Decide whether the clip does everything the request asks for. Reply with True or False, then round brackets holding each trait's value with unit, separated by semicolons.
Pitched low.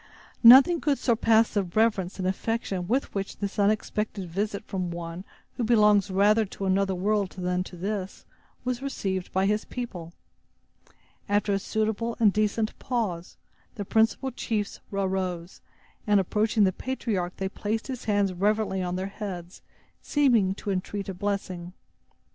False (200 Hz)